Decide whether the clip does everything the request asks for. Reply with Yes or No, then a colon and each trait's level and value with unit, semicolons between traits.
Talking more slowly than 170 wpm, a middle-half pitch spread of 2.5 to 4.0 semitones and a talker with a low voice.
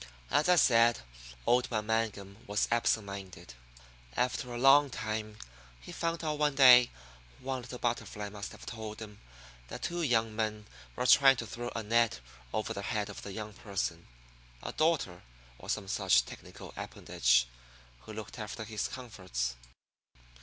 Yes: average, 160 wpm; average, 3.3 semitones; low, 110 Hz